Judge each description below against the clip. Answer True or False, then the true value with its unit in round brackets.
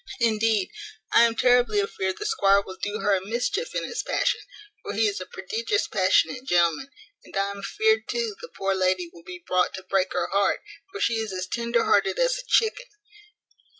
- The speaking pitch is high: True (215 Hz)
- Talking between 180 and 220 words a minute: True (200 wpm)